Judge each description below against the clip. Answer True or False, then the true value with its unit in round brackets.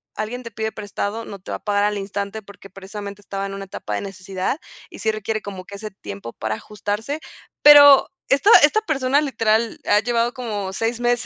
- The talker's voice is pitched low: False (210 Hz)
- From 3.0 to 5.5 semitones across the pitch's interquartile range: True (3.3 semitones)